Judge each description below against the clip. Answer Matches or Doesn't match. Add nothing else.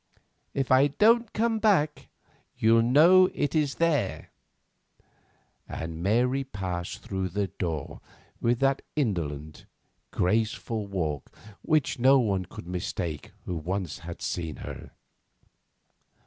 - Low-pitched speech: Matches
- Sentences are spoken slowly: Matches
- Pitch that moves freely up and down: Matches